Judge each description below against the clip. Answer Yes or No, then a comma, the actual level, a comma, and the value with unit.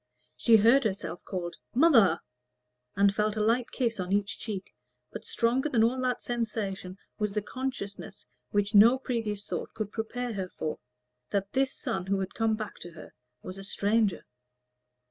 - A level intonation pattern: No, average, 3.2 semitones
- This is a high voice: Yes, high, 210 Hz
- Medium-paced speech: Yes, average, 165 wpm